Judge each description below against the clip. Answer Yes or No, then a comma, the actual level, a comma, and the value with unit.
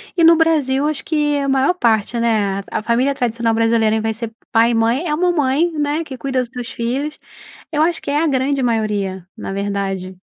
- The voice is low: No, very high, 250 Hz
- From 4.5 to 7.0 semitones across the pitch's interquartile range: Yes, average, 4.9 semitones